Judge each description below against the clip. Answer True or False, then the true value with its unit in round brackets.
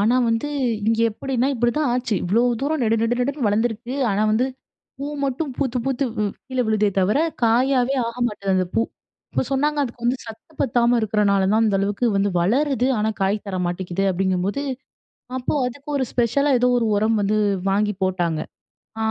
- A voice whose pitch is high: True (230 Hz)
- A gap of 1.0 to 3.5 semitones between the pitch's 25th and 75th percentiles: False (3.9 semitones)